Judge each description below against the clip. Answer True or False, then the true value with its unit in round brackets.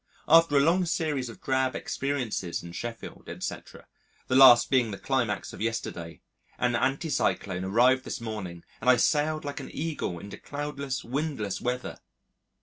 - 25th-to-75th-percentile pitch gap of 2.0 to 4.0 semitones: False (4.5 semitones)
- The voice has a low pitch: True (130 Hz)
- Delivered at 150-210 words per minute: True (155 wpm)